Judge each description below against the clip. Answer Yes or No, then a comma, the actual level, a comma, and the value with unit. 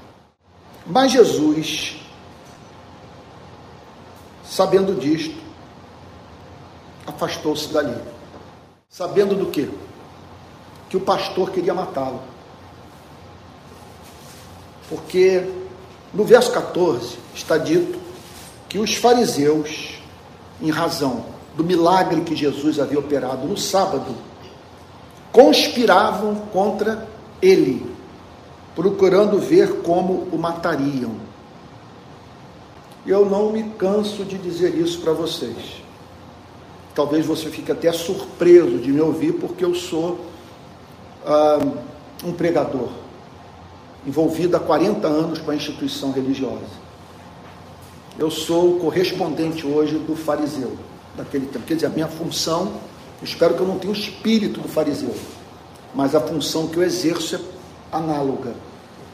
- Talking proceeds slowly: Yes, slow, 105 wpm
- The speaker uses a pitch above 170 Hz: No, medium, 165 Hz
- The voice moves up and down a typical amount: Yes, average, 4.9 semitones